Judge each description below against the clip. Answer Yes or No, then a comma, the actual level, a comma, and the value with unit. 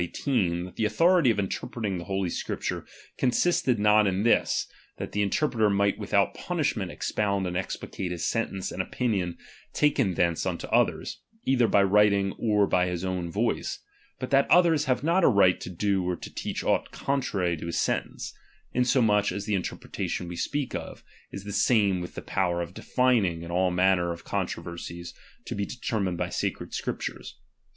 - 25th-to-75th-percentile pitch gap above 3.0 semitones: Yes, average, 4.7 semitones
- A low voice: Yes, low, 100 Hz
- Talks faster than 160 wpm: Yes, average, 180 wpm